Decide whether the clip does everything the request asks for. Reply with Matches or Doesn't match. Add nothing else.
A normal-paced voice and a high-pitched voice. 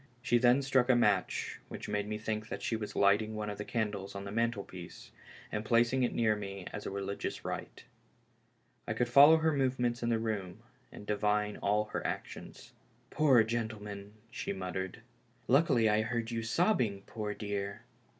Doesn't match